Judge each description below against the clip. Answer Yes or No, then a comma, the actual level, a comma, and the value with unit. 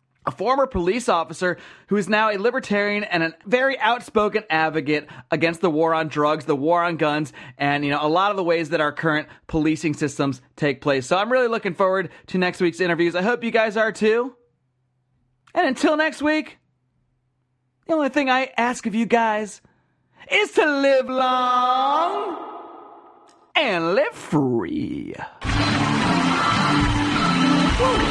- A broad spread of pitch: Yes, wide, 8.6 semitones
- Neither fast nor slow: Yes, average, 155 wpm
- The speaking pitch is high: Yes, high, 195 Hz